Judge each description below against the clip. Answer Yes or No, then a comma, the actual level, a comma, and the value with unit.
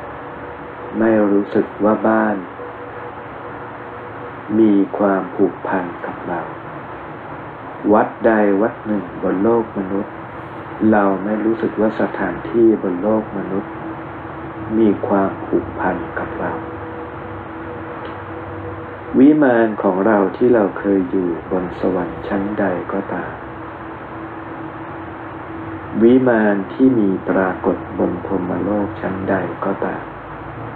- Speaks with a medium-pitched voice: No, low, 105 Hz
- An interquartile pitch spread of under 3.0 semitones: Yes, narrow, 2.4 semitones